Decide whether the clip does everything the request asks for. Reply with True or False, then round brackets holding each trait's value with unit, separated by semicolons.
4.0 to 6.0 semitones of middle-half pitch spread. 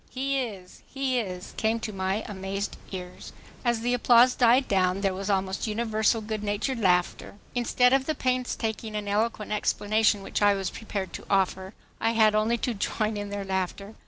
False (3.2 semitones)